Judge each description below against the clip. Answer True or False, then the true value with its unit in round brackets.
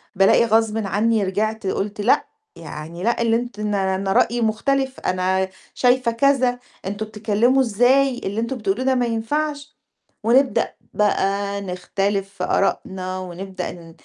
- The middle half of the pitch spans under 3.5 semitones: False (4.0 semitones)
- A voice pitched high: True (215 Hz)